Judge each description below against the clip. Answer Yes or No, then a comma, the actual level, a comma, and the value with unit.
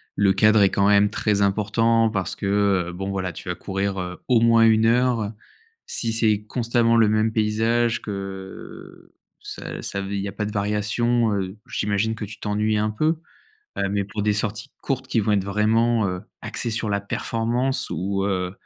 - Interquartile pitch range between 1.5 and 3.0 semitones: Yes, narrow, 2.4 semitones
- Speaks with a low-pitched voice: Yes, low, 105 Hz